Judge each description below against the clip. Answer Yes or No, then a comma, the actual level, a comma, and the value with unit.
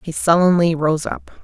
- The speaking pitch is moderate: Yes, medium, 165 Hz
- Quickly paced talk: No, average, 165 wpm